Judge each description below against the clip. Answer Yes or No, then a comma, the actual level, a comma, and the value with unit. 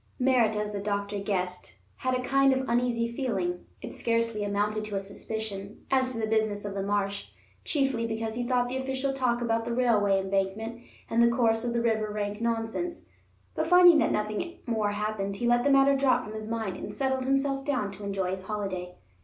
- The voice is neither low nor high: No, high, 225 Hz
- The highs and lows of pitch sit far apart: No, average, 3.7 semitones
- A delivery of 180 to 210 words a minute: Yes, average, 195 wpm